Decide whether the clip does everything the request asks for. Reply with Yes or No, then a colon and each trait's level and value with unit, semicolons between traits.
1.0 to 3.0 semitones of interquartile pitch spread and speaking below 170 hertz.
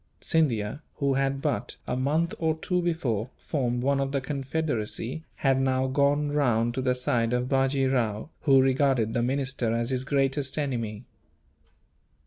Yes: narrow, 2.5 semitones; low, 135 Hz